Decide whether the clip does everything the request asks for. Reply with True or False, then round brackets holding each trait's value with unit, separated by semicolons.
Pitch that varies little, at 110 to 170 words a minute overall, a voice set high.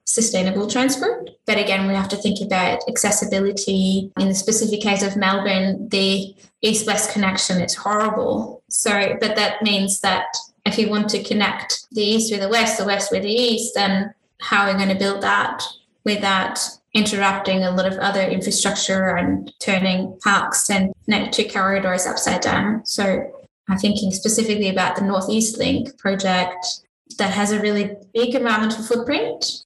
True (2.1 semitones; 165 wpm; 200 Hz)